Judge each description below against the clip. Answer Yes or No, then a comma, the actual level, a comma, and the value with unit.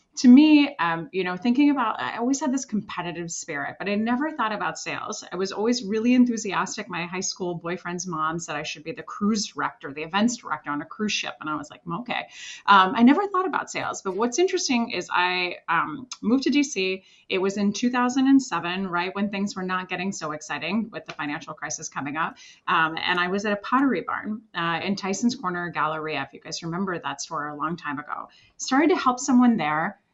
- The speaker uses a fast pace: Yes, fast, 215 wpm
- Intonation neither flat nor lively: No, wide, 6.3 semitones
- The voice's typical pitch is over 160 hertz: Yes, high, 190 Hz